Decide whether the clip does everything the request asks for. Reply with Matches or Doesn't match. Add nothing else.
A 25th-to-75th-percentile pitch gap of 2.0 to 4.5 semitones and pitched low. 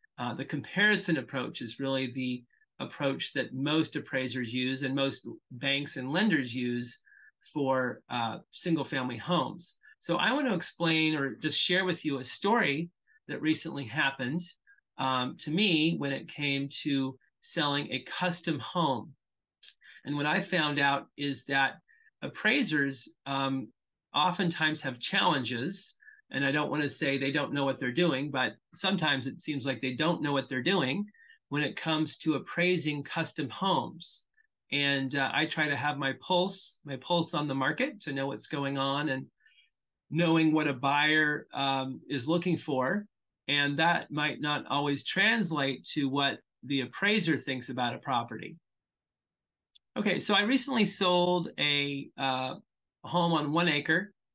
Doesn't match